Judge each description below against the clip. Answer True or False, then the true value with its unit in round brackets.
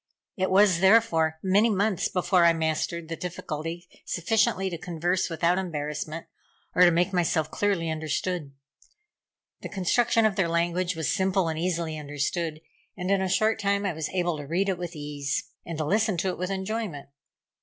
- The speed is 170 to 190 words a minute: True (175 wpm)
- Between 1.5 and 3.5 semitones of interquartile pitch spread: True (3.1 semitones)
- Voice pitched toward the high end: False (175 Hz)